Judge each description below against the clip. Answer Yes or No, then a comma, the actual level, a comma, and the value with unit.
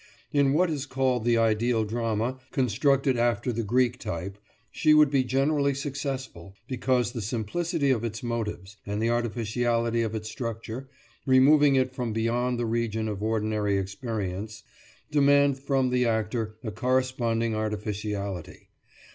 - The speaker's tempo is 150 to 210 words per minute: No, average, 140 wpm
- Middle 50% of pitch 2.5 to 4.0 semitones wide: Yes, average, 3.3 semitones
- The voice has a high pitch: No, low, 120 Hz